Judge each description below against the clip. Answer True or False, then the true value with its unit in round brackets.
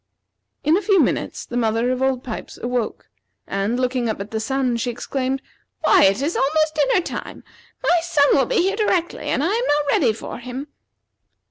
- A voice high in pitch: True (265 Hz)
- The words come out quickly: False (195 wpm)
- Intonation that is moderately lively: True (4.7 semitones)